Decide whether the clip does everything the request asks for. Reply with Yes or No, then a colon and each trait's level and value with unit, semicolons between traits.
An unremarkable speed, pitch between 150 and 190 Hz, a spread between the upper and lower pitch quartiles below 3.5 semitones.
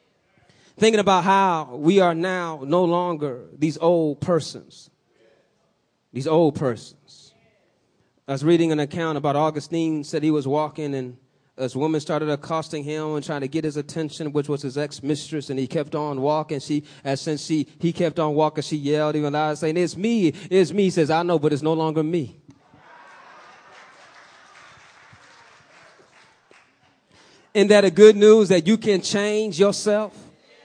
Yes: average, 160 wpm; medium, 155 Hz; average, 2.9 semitones